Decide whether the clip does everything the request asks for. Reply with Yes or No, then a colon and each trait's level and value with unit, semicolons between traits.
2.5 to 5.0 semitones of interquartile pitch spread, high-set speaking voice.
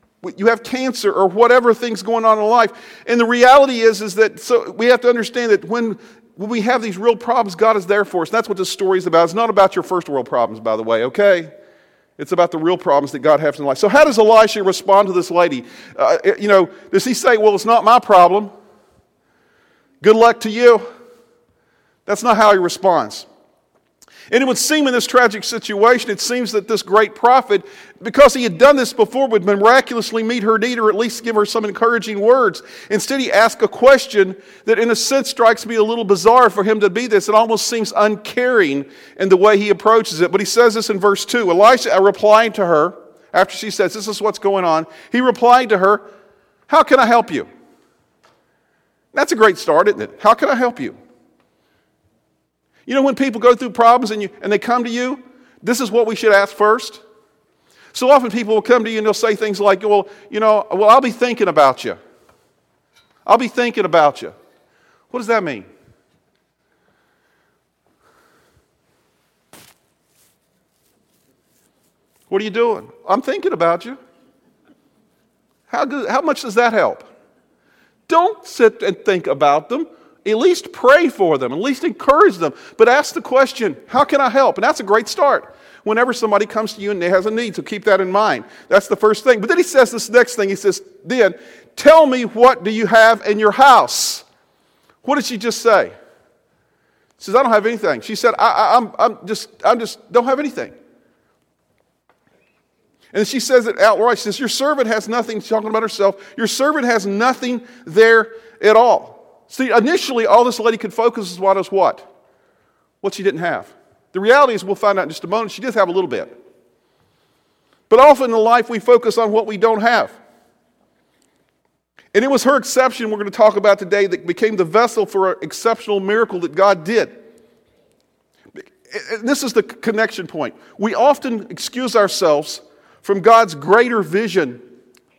Yes: average, 3.2 semitones; high, 225 Hz